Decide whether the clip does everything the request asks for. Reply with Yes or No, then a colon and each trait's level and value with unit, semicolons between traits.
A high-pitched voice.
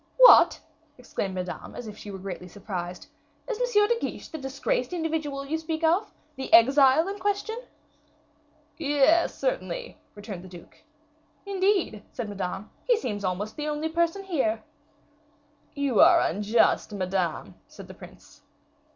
Yes: very high, 280 Hz